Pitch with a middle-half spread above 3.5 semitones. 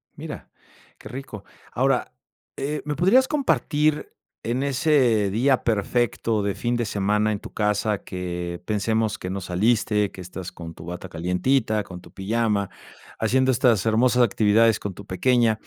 Yes: average, 4.1 semitones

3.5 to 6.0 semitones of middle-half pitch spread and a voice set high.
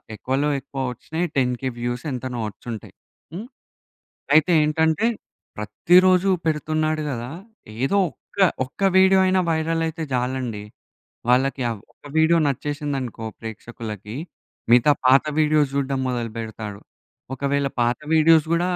No: average, 4.6 semitones; medium, 140 Hz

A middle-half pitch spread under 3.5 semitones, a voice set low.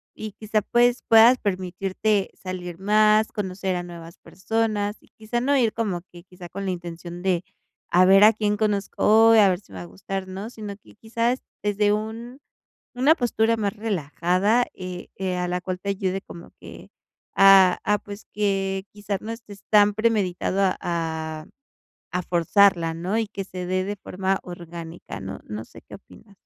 No: average, 3.1 semitones; high, 195 Hz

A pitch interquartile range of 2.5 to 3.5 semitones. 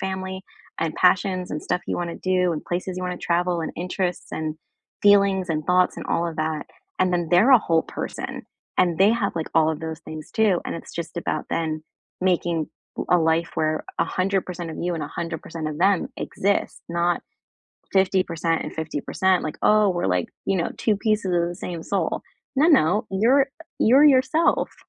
Yes: average, 2.8 semitones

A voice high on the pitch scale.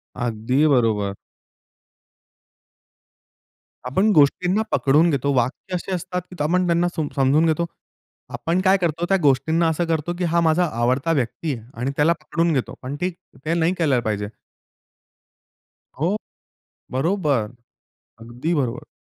No: medium, 155 Hz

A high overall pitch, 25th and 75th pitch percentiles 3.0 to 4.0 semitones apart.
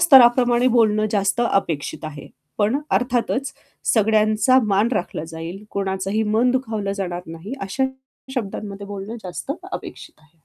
Yes: high, 210 Hz; average, 3.7 semitones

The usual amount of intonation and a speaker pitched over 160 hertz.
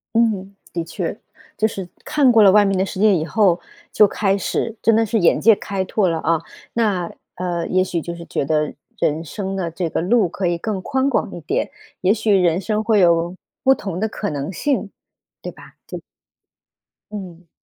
Yes: average, 3.9 semitones; high, 190 Hz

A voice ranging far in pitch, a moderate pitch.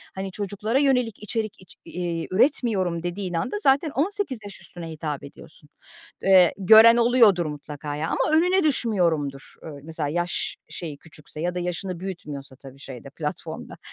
Yes: wide, 6.5 semitones; medium, 180 Hz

